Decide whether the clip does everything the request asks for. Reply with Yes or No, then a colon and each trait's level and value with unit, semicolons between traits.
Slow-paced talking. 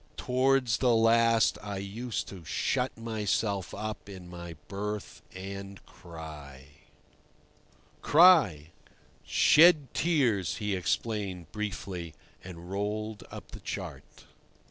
Yes: slow, 100 wpm